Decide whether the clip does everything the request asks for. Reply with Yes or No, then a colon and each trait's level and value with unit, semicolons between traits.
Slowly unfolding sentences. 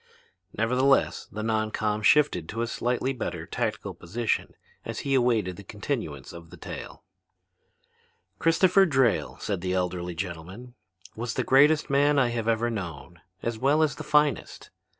No: average, 150 wpm